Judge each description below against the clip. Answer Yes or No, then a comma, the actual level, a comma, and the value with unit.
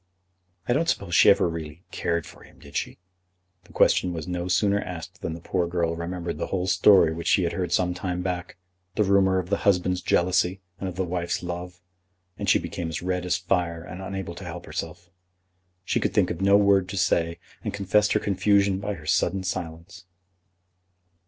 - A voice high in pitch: No, very low, 90 Hz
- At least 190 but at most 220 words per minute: Yes, average, 200 wpm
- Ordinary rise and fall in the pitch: No, narrow, 1.9 semitones